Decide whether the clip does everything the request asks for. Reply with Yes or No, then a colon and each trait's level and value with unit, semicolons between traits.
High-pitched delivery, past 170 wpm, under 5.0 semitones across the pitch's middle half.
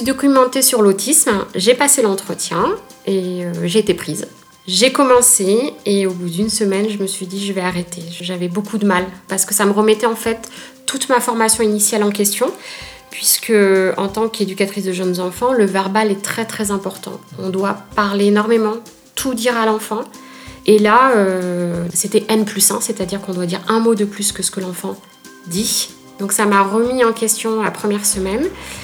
Yes: high, 205 Hz; average, 190 wpm; average, 3.1 semitones